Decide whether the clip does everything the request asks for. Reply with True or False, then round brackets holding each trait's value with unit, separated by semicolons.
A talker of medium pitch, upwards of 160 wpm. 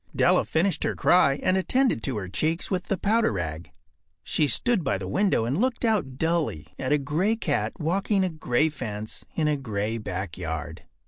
True (150 Hz; 185 wpm)